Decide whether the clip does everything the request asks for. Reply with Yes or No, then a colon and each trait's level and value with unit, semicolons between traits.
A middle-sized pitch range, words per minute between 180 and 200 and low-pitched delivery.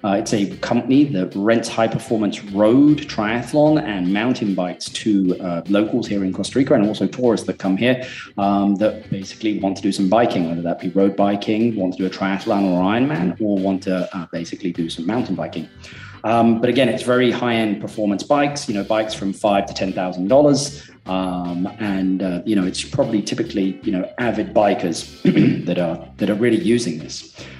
Yes: average, 3.7 semitones; average, 195 wpm; low, 100 Hz